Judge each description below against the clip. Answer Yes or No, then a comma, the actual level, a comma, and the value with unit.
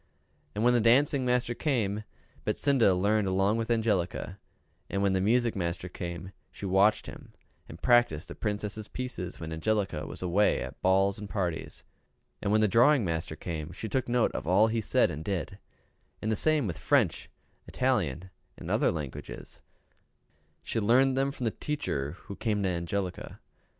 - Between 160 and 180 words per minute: Yes, average, 170 wpm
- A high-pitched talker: No, low, 105 Hz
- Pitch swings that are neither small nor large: Yes, average, 4.6 semitones